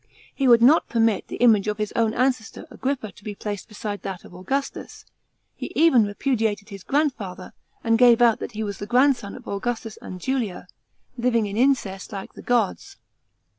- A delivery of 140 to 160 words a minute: No, average, 180 wpm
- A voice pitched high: Yes, high, 225 Hz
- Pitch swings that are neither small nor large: Yes, average, 3.4 semitones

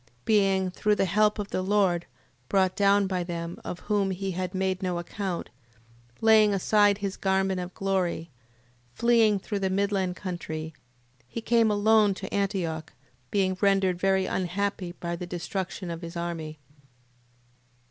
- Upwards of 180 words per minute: No, average, 145 wpm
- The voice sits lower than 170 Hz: No, high, 190 Hz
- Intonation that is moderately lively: No, narrow, 2.2 semitones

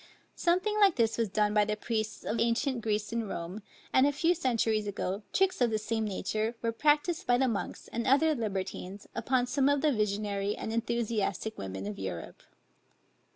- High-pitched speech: Yes, high, 225 Hz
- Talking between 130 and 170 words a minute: No, average, 185 wpm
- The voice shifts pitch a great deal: No, average, 4.0 semitones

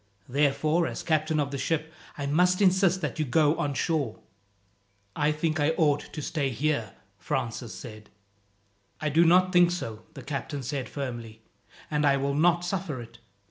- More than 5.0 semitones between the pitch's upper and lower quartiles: No, average, 3.3 semitones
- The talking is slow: No, average, 170 wpm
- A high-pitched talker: No, medium, 150 Hz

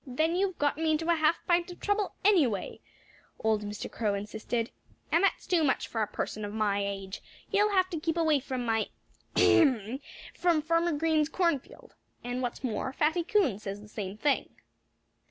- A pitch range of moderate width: No, wide, 7.6 semitones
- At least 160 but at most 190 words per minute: Yes, average, 180 wpm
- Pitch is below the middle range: No, very high, 290 Hz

